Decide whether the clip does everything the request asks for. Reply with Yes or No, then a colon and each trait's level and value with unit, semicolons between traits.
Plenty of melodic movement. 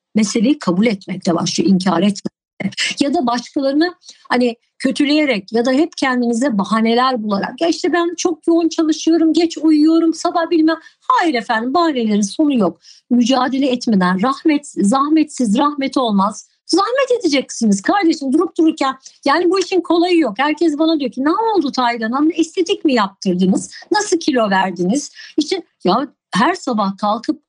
Yes: wide, 6.3 semitones